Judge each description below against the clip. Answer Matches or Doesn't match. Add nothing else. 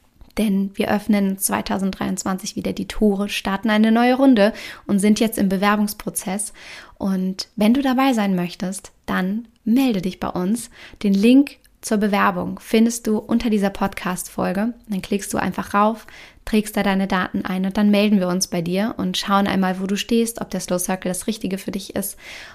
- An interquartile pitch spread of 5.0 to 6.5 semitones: Doesn't match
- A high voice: Matches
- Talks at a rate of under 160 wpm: Doesn't match